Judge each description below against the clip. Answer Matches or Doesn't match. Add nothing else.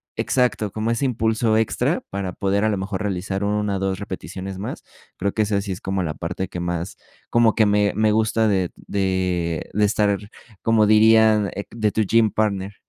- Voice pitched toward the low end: Matches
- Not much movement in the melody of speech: Matches